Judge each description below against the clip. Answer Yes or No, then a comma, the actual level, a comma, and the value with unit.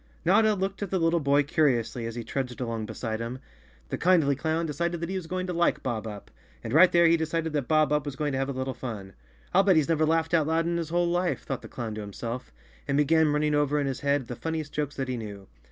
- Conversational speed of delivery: No, fast, 265 wpm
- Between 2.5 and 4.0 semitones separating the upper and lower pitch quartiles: No, average, 4.6 semitones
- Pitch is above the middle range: No, medium, 150 Hz